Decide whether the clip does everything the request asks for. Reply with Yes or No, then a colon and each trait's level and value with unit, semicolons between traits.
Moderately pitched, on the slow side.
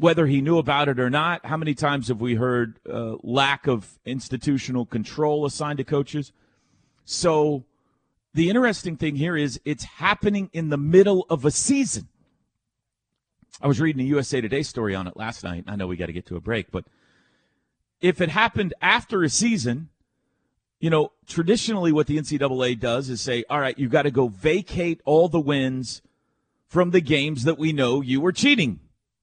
No: medium, 145 Hz; average, 185 wpm